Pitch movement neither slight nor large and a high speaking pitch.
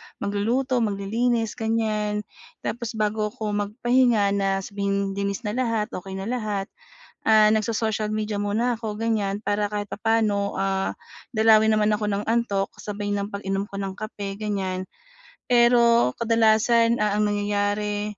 No: narrow, 1.9 semitones; high, 210 Hz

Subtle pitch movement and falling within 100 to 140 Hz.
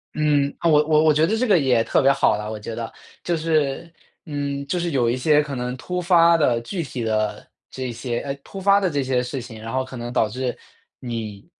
No: average, 4.8 semitones; low, 135 Hz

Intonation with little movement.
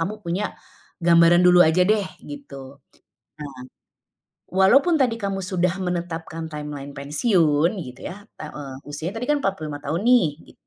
No: average, 4.7 semitones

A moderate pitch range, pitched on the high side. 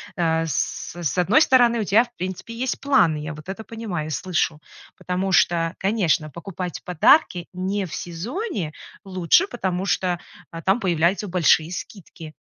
No: average, 3.9 semitones; medium, 180 Hz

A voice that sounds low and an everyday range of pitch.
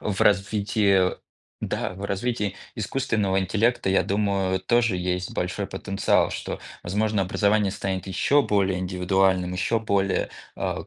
No: very low, 95 Hz; narrow, 1.9 semitones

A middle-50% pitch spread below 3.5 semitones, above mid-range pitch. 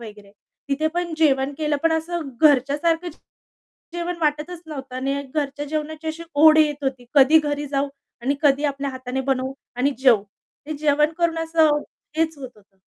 Yes: average, 2.8 semitones; very high, 290 Hz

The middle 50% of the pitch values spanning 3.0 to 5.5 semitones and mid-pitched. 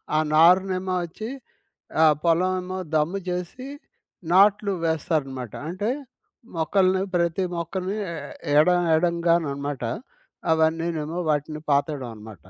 Yes: average, 3.3 semitones; medium, 170 Hz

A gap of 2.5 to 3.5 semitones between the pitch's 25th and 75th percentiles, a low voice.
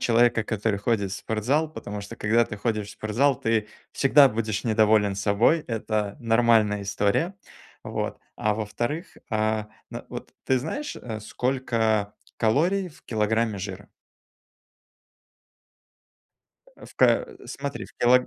Yes: average, 2.9 semitones; low, 110 Hz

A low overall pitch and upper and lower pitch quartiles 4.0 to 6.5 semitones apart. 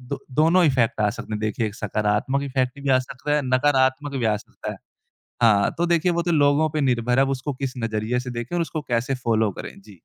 Yes: low, 130 Hz; average, 4.3 semitones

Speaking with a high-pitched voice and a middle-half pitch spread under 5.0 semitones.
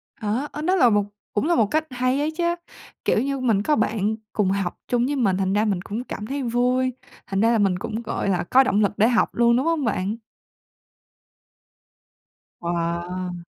Yes: high, 225 Hz; average, 4.6 semitones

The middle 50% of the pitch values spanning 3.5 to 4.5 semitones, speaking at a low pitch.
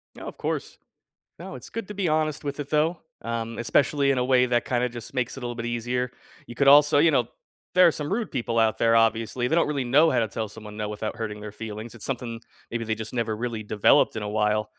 Yes: average, 4.0 semitones; low, 120 Hz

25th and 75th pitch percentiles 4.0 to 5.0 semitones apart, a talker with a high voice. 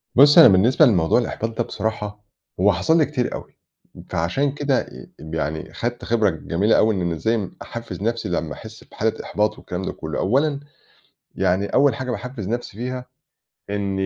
No: average, 4.7 semitones; low, 110 Hz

